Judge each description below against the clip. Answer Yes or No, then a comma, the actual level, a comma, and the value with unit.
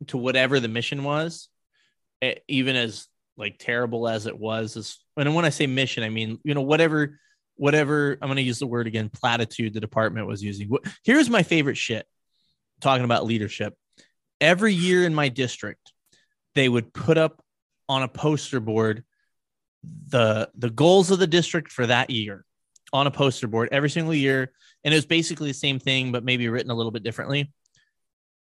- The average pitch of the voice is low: Yes, low, 130 Hz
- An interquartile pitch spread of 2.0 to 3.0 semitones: No, average, 4.6 semitones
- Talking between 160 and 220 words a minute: Yes, average, 180 wpm